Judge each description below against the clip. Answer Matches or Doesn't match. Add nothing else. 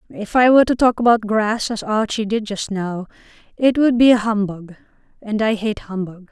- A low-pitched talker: Doesn't match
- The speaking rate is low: Doesn't match